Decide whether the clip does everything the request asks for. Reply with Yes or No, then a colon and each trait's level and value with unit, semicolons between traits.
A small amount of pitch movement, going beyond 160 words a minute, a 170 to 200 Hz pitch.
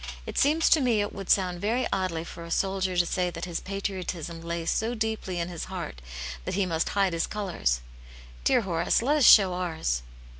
No: average, 3.3 semitones; average, 200 wpm; medium, 185 Hz